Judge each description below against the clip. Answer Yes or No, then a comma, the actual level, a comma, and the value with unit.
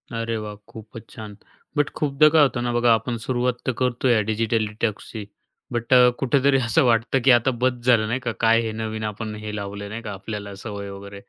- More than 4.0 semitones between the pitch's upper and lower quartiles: No, average, 2.7 semitones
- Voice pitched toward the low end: Yes, low, 115 Hz